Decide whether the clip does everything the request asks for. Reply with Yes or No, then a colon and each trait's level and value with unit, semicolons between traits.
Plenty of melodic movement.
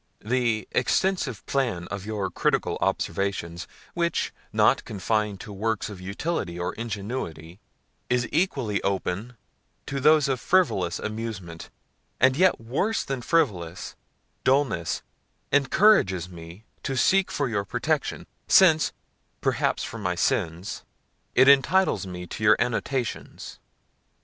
Yes: wide, 6.5 semitones